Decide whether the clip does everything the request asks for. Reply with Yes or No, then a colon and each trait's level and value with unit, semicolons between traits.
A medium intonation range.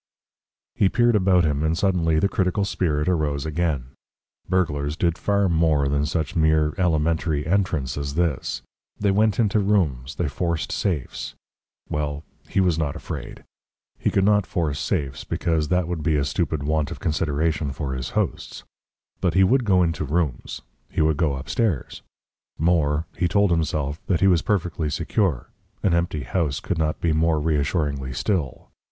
Yes: average, 3.7 semitones